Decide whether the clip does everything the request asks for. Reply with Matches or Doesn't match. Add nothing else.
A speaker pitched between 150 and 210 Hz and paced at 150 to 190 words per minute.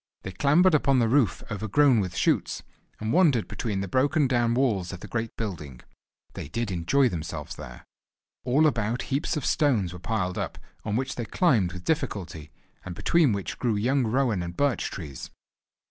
Doesn't match